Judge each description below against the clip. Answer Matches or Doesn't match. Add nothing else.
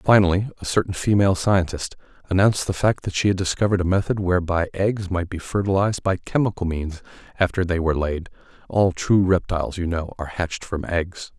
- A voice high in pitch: Doesn't match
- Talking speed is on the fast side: Doesn't match